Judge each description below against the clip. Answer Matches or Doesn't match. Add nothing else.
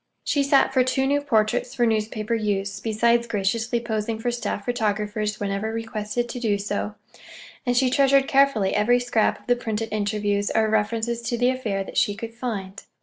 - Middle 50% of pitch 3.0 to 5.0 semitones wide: Doesn't match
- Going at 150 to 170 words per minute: Doesn't match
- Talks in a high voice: Matches